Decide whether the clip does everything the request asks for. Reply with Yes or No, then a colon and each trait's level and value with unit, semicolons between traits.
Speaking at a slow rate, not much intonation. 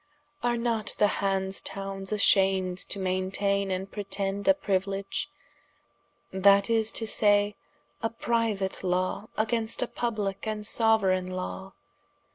Yes: slow, 120 wpm; narrow, 2.3 semitones